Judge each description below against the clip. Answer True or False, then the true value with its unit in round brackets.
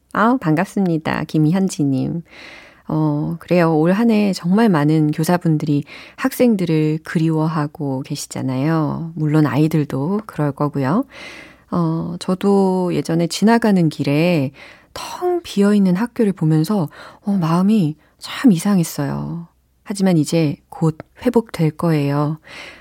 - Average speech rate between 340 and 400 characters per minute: False (255 characters per minute)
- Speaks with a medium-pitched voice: True (165 Hz)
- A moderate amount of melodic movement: True (4.5 semitones)